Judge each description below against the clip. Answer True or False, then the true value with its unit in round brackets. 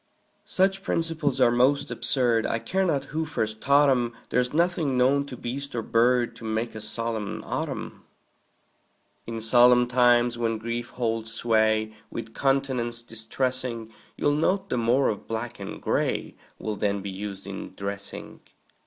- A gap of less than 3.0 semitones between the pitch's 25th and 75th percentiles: False (3.3 semitones)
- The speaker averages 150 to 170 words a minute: True (155 wpm)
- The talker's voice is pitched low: True (120 Hz)